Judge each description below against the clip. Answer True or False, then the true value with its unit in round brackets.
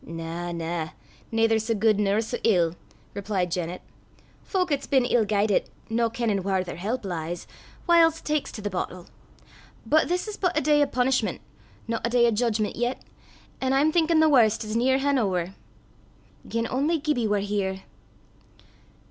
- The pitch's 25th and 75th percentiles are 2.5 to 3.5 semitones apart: False (5.6 semitones)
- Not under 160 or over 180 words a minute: True (165 wpm)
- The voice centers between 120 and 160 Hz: False (225 Hz)